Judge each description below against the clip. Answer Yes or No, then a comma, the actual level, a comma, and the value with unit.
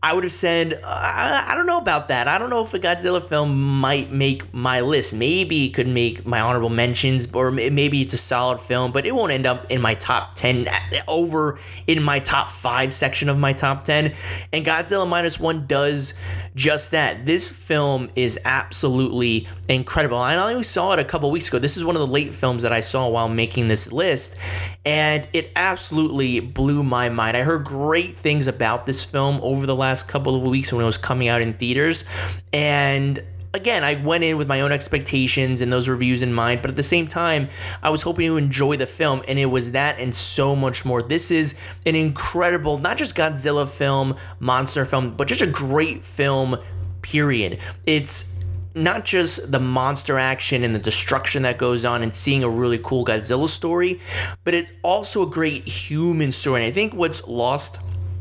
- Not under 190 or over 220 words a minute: Yes, average, 200 wpm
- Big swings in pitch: No, average, 4.0 semitones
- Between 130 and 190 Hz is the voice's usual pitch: Yes, low, 135 Hz